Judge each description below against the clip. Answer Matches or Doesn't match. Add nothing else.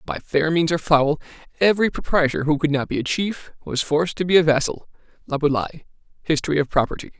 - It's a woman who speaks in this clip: Doesn't match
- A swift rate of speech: Doesn't match